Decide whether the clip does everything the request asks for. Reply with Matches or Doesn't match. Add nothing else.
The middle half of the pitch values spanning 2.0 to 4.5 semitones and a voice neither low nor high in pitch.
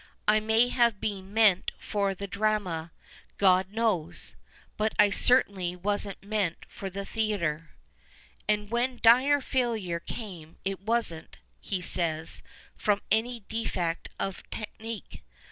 Doesn't match